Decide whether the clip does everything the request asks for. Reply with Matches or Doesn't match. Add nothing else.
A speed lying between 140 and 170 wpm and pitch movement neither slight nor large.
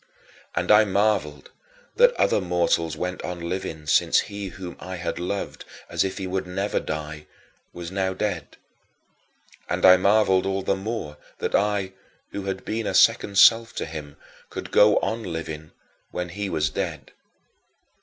Matches